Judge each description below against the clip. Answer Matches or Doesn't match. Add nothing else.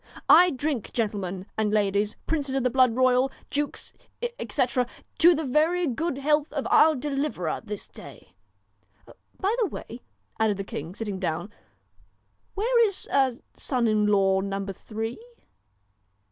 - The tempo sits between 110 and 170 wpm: Matches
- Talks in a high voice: Matches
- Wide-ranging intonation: Matches